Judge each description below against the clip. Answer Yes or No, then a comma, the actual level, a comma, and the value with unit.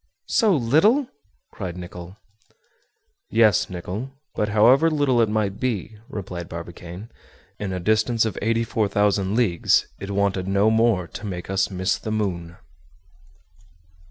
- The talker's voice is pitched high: No, low, 105 Hz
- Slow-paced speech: Yes, slow, 130 wpm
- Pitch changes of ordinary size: Yes, average, 3.6 semitones